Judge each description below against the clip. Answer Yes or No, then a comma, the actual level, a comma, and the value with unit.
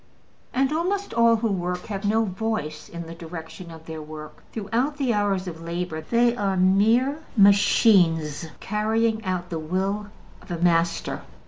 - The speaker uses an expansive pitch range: No, average, 5.0 semitones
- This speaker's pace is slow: No, average, 155 wpm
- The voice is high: Yes, high, 195 Hz